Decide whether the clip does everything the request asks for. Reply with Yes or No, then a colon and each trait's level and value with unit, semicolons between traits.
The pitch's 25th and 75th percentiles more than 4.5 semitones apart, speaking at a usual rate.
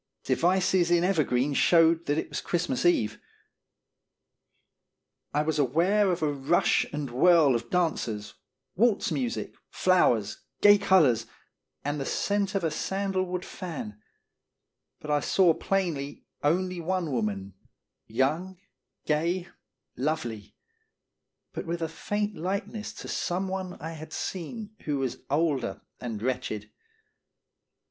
No: average, 5.3 semitones; slow, 125 wpm